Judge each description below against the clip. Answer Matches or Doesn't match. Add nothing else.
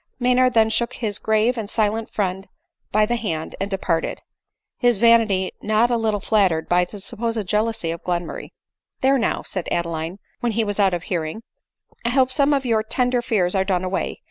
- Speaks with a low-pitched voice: Doesn't match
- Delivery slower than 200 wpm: Doesn't match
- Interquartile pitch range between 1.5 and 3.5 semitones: Doesn't match